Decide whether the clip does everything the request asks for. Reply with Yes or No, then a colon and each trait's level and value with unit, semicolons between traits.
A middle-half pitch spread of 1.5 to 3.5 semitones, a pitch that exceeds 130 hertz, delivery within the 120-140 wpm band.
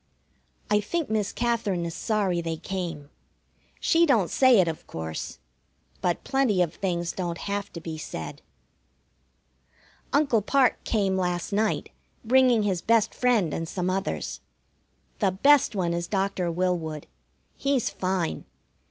No: average, 4.7 semitones; high, 190 Hz; slow, 135 wpm